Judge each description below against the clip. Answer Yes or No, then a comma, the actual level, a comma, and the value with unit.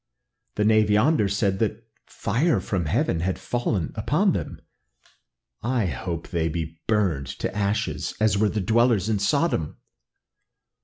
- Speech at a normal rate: Yes, average, 145 wpm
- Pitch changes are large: No, average, 3.8 semitones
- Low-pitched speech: Yes, low, 105 Hz